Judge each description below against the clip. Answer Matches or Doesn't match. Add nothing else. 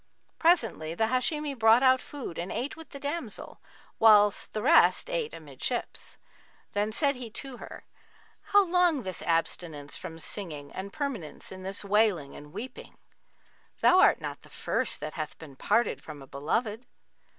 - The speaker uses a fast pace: Doesn't match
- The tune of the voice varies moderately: Doesn't match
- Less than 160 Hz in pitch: Doesn't match